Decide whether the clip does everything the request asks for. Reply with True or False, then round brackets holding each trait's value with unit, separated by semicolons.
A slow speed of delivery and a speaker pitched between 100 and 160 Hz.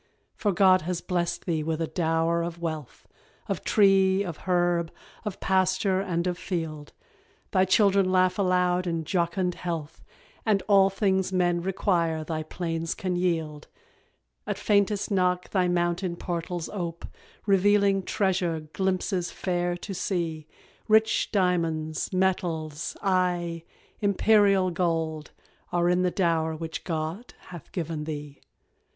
False (130 wpm; 180 Hz)